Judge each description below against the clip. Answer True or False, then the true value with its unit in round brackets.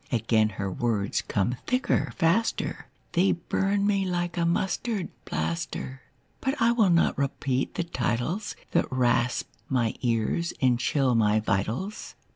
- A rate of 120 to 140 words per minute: True (135 wpm)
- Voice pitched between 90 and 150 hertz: True (140 Hz)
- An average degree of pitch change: False (8.2 semitones)